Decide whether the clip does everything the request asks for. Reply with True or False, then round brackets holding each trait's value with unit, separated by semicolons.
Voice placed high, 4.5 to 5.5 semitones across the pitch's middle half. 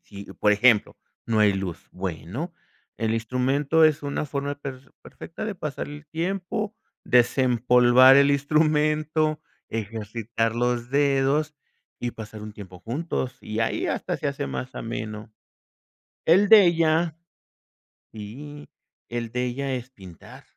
False (130 Hz; 5.2 semitones)